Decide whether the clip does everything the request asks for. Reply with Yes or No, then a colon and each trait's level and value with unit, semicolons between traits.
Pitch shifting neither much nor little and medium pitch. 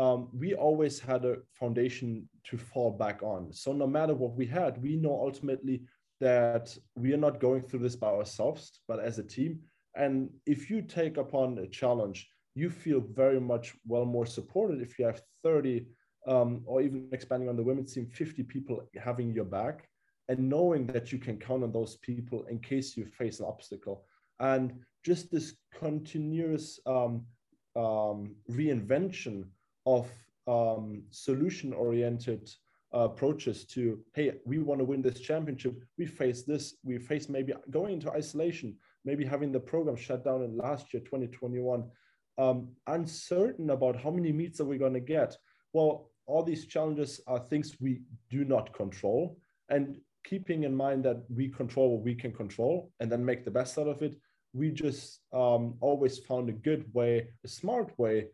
No: average, 3.5 semitones; low, 130 Hz